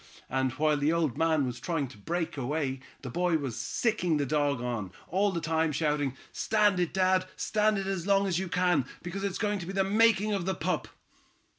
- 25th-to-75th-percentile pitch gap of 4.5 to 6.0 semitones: Yes, average, 5.1 semitones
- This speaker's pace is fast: Yes, fast, 210 wpm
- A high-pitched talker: No, medium, 170 Hz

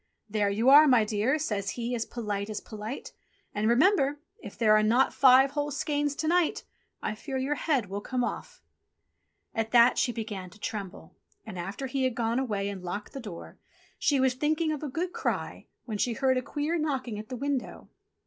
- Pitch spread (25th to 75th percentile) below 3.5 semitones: No, average, 4.7 semitones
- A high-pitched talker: Yes, high, 245 Hz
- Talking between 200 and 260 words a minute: Yes, fast, 205 wpm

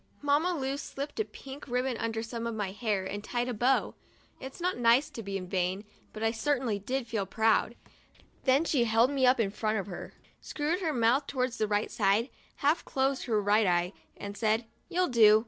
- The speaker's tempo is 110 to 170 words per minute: No, average, 200 wpm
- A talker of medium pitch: No, high, 235 Hz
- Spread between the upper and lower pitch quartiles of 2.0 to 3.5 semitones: No, average, 4.2 semitones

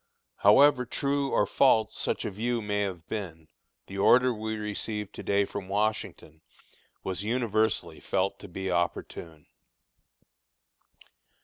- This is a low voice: Yes, low, 105 Hz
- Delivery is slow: Yes, slow, 125 wpm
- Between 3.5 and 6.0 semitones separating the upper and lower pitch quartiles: No, average, 2.7 semitones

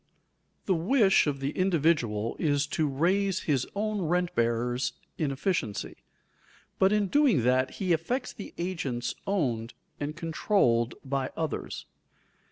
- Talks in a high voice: No, medium, 155 Hz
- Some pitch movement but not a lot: No, wide, 6.6 semitones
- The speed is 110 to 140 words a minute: Yes, slow, 135 wpm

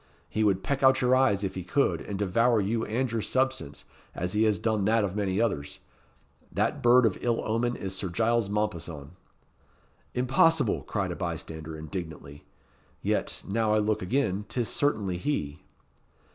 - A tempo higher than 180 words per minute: No, average, 165 wpm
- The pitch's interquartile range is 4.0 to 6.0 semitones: Yes, average, 4.5 semitones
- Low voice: Yes, low, 105 Hz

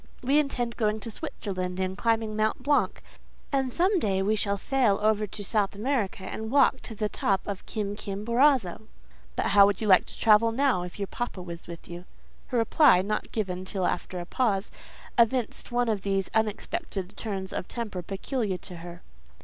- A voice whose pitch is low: No, high, 210 Hz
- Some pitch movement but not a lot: Yes, average, 3.6 semitones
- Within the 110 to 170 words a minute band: No, average, 180 wpm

